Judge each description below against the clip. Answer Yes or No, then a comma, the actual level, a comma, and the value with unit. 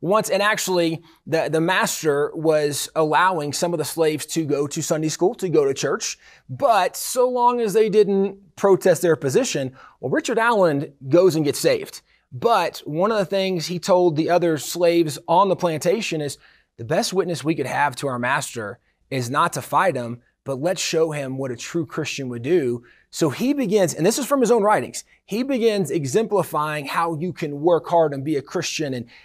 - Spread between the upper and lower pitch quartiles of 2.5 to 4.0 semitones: No, average, 4.8 semitones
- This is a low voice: No, medium, 165 Hz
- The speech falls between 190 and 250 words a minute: Yes, average, 200 wpm